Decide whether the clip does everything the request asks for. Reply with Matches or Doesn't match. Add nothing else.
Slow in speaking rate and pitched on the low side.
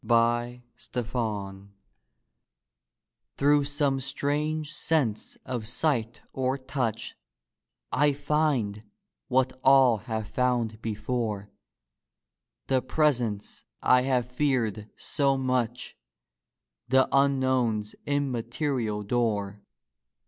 Matches